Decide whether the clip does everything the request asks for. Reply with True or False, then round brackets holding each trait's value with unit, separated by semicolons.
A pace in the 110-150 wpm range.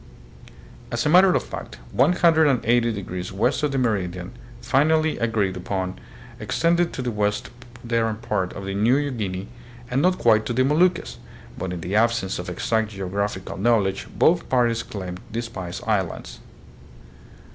True (145 wpm)